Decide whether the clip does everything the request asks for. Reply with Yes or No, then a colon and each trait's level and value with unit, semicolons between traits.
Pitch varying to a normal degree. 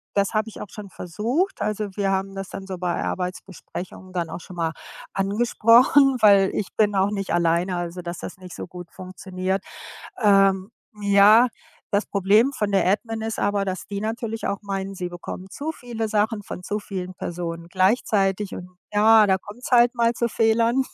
Yes: average, 3.0 semitones